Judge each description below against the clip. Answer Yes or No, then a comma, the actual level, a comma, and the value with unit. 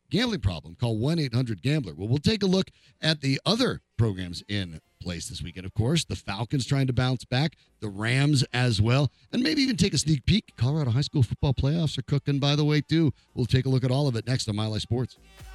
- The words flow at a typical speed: No, fast, 240 wpm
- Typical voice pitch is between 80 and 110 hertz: No, low, 130 Hz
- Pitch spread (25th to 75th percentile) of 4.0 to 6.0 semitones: Yes, average, 5.3 semitones